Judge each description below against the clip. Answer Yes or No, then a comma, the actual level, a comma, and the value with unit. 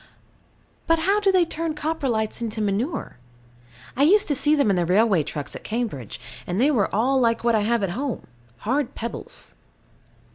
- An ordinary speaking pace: Yes, average, 180 wpm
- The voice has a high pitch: Yes, high, 235 Hz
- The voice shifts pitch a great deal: Yes, wide, 6.3 semitones